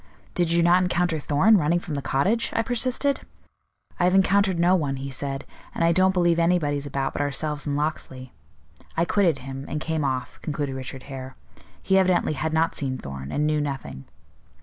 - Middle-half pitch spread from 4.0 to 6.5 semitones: Yes, average, 4.4 semitones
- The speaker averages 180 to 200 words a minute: Yes, average, 190 wpm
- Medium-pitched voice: Yes, medium, 155 Hz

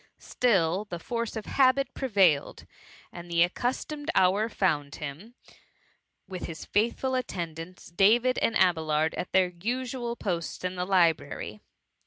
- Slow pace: Yes, slow, 130 wpm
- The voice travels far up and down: Yes, wide, 5.8 semitones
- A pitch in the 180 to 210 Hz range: Yes, high, 190 Hz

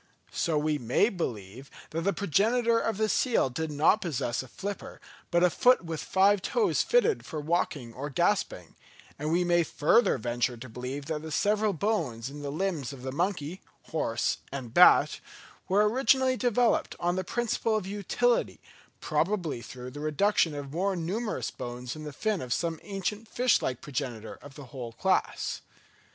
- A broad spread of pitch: Yes, wide, 7.1 semitones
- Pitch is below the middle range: No, medium, 165 Hz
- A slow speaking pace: No, average, 170 wpm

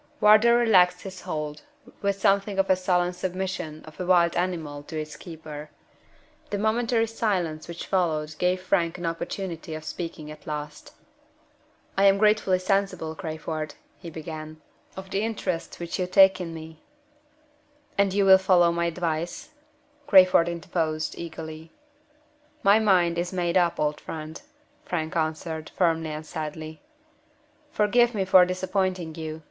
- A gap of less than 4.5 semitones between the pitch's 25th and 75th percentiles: Yes, average, 3.4 semitones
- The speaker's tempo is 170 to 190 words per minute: No, average, 145 wpm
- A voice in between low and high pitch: Yes, medium, 175 Hz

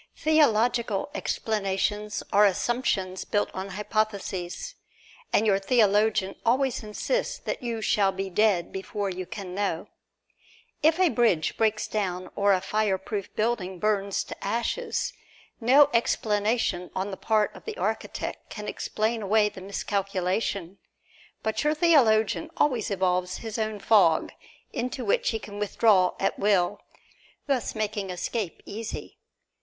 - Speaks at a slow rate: Yes, slow, 130 wpm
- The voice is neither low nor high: No, high, 210 Hz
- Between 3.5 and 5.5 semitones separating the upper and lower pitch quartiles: No, average, 2.9 semitones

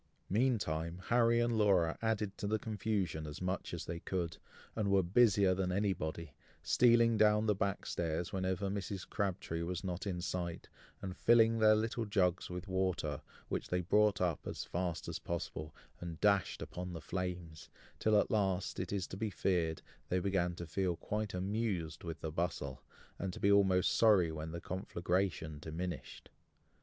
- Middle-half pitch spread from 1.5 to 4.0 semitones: Yes, average, 3.3 semitones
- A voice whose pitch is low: Yes, very low, 95 Hz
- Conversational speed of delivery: Yes, average, 170 wpm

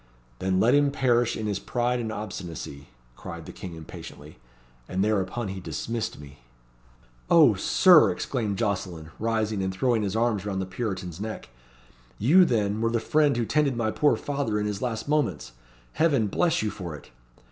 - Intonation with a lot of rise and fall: No, average, 4.2 semitones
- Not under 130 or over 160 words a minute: No, average, 170 wpm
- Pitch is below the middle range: Yes, low, 110 Hz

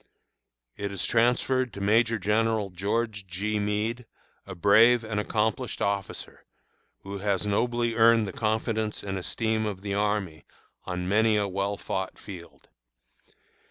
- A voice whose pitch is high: No, low, 105 Hz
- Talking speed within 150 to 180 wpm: No, slow, 135 wpm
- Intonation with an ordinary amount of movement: No, narrow, 2.2 semitones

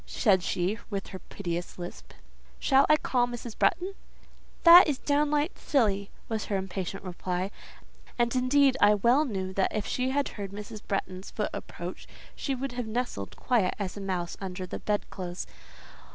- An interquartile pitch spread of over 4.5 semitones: Yes, average, 5.3 semitones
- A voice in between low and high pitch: No, high, 210 Hz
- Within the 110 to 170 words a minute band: Yes, average, 165 wpm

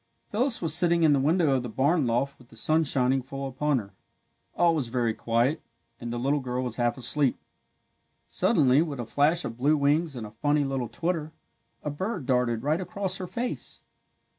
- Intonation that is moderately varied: Yes, average, 4.5 semitones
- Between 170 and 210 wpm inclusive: Yes, average, 195 wpm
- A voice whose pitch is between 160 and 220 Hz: No, medium, 140 Hz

